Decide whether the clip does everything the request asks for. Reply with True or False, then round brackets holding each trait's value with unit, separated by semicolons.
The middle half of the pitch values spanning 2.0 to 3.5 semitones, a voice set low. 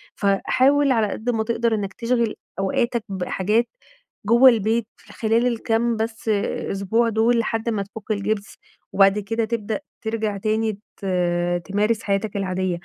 False (2.5 semitones; 220 Hz)